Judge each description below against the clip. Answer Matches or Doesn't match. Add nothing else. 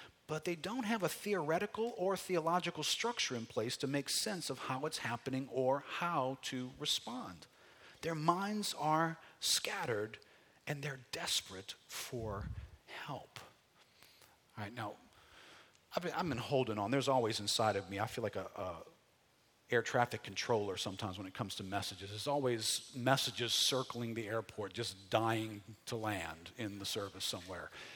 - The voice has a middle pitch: Doesn't match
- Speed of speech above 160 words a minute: Doesn't match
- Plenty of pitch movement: Matches